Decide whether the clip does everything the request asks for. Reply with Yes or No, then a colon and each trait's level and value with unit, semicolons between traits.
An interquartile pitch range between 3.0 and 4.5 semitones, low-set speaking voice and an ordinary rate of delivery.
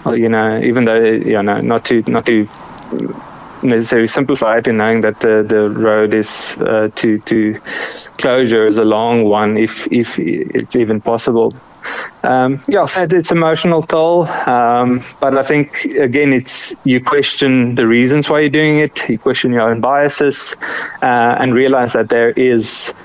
Yes: average, 3.9 semitones; low, 120 Hz; average, 170 wpm